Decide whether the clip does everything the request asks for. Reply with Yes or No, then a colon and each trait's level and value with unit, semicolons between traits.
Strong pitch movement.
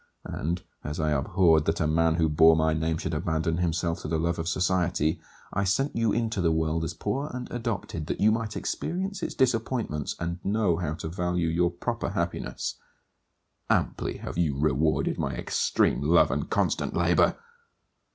No: average, 3.6 semitones